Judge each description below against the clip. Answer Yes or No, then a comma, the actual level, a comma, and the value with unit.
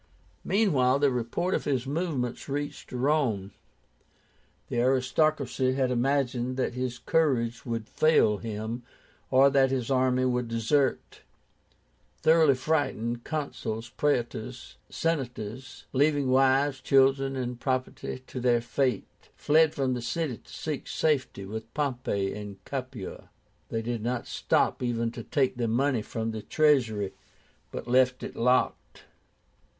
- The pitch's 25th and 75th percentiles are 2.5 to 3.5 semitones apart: Yes, average, 2.9 semitones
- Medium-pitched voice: No, low, 130 Hz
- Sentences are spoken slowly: Yes, slow, 130 wpm